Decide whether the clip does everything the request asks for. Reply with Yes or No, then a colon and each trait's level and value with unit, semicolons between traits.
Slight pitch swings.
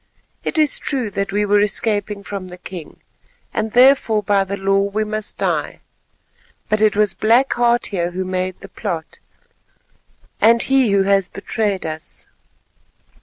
Yes: narrow, 2.3 semitones